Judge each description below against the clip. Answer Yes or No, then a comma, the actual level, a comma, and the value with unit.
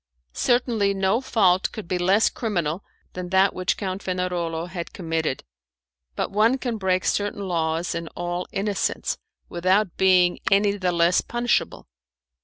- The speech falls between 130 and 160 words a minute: Yes, average, 140 wpm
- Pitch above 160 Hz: Yes, medium, 185 Hz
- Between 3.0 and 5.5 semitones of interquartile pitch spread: No, narrow, 2.6 semitones